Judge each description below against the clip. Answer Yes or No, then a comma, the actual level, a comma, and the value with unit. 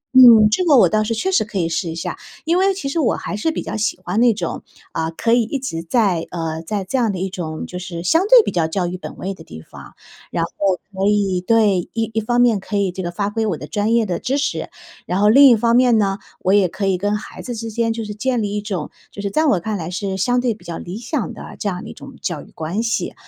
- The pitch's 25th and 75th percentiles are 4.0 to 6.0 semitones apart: Yes, average, 4.4 semitones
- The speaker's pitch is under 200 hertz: No, high, 205 Hz